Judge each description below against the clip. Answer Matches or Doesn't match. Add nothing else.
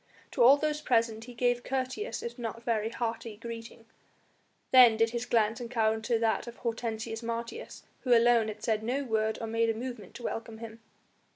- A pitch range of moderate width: Doesn't match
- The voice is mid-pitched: Doesn't match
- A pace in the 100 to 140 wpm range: Doesn't match